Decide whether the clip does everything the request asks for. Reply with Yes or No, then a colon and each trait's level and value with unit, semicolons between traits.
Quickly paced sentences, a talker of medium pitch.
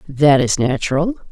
No: slow, 135 wpm; medium, 150 Hz